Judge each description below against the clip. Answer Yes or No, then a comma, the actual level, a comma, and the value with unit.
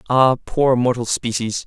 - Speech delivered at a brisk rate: No, average, 145 wpm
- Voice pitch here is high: No, low, 125 Hz